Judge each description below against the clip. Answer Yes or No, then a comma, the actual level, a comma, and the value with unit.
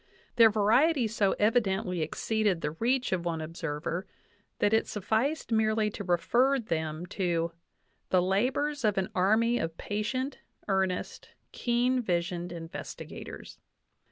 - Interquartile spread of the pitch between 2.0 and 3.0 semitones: No, average, 4.9 semitones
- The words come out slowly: Yes, slow, 130 wpm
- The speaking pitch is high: Yes, high, 205 Hz